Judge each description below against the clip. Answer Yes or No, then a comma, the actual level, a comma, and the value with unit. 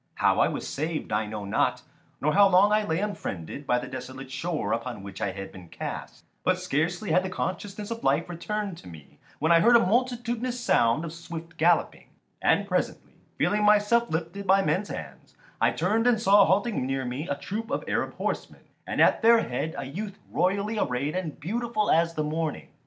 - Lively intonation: Yes, wide, 7.2 semitones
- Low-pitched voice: No, medium, 170 Hz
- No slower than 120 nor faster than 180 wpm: No, average, 195 wpm